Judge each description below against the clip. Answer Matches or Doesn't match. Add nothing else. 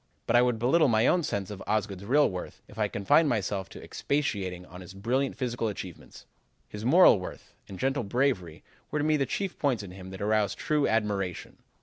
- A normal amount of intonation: Doesn't match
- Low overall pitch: Matches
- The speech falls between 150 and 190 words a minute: Doesn't match